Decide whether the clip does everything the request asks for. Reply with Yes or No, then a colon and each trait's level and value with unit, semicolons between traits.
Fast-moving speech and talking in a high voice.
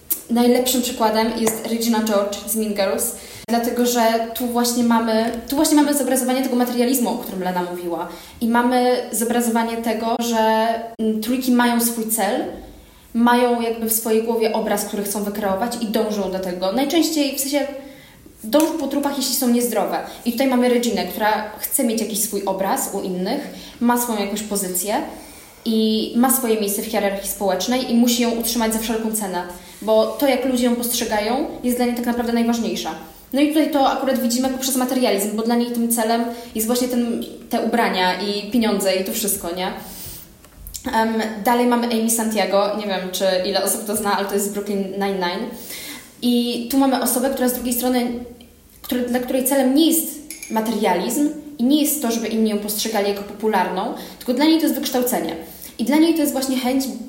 Yes: fast, 185 wpm; high, 235 Hz